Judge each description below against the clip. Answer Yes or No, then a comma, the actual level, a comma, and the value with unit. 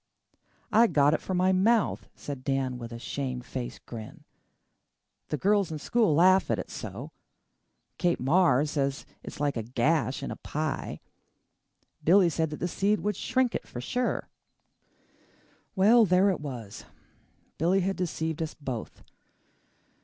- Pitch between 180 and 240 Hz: No, medium, 160 Hz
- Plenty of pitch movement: Yes, wide, 5.8 semitones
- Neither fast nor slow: Yes, average, 145 wpm